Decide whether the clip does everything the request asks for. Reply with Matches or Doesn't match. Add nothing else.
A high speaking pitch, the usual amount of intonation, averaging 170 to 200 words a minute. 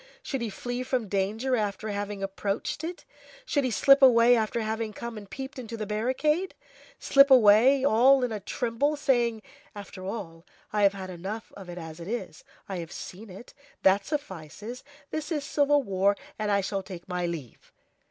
Matches